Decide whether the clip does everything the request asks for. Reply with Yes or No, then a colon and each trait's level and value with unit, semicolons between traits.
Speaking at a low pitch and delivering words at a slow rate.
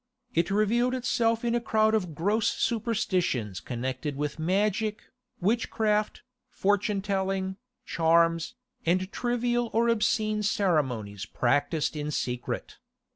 No: high, 195 Hz; slow, 110 wpm